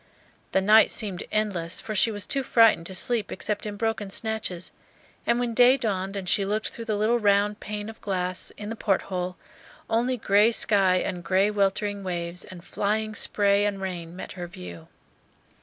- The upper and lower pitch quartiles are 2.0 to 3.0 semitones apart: Yes, average, 2.7 semitones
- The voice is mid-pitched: No, high, 205 Hz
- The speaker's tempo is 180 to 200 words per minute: Yes, average, 185 wpm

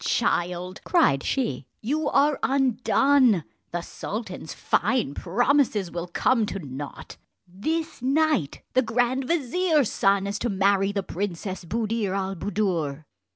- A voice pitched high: Yes, high, 210 Hz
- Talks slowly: Yes, slow, 125 wpm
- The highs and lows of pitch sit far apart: Yes, wide, 6.2 semitones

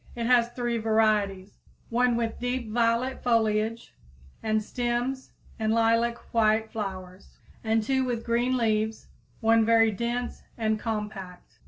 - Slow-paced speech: Yes, slow, 130 wpm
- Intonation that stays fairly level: Yes, narrow, 1.7 semitones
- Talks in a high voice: Yes, high, 225 Hz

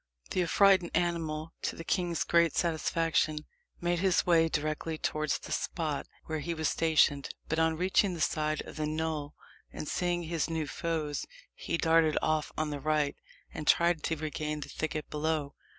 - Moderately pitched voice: Yes, medium, 160 Hz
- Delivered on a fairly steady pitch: Yes, narrow, 1.7 semitones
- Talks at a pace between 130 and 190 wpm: Yes, average, 170 wpm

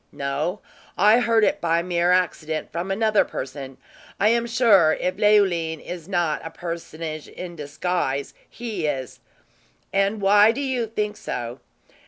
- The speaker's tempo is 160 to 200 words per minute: No, average, 145 wpm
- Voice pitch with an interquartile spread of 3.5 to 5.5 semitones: Yes, average, 5.0 semitones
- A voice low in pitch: No, medium, 180 Hz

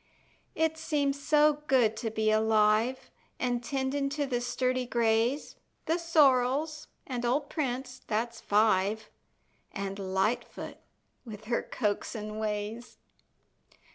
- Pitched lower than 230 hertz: No, high, 245 Hz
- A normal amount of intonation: Yes, average, 4.3 semitones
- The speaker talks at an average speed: No, slow, 110 wpm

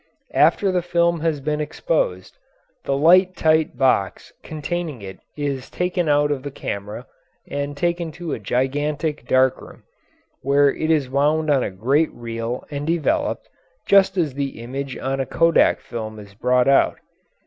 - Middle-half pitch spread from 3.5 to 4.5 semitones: Yes, average, 3.9 semitones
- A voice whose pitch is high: No, medium, 145 Hz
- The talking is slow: No, average, 160 wpm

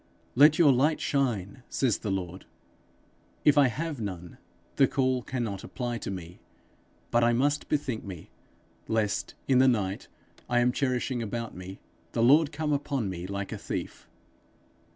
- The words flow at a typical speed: Yes, average, 155 wpm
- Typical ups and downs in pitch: No, wide, 5.7 semitones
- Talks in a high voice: No, low, 120 Hz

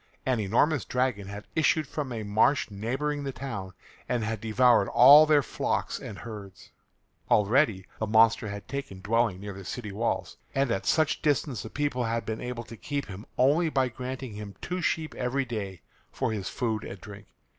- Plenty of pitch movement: No, average, 4.7 semitones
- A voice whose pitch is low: Yes, low, 115 Hz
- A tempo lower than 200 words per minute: Yes, average, 185 wpm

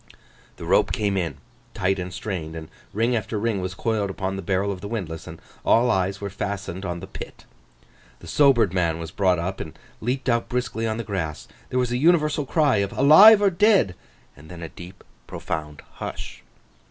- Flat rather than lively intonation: No, average, 5.2 semitones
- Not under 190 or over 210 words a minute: Yes, average, 195 wpm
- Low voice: Yes, low, 100 Hz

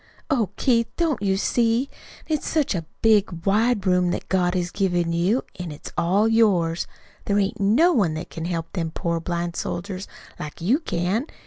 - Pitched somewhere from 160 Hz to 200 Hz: Yes, high, 190 Hz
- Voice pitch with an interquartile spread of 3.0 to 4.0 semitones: No, average, 4.7 semitones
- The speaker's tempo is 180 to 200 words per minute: Yes, average, 185 wpm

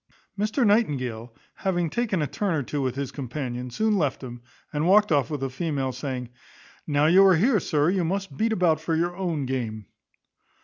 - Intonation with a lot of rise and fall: Yes, wide, 6.4 semitones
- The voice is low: No, medium, 155 Hz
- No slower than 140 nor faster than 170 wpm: No, average, 190 wpm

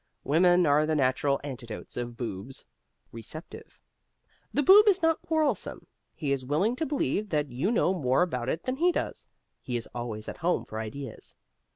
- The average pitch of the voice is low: No, medium, 145 Hz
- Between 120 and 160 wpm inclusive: No, average, 175 wpm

